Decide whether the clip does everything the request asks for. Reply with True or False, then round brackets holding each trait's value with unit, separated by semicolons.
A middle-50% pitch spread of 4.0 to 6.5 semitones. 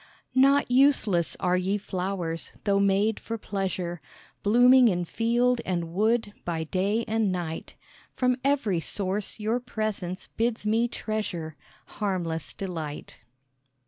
True (4.3 semitones)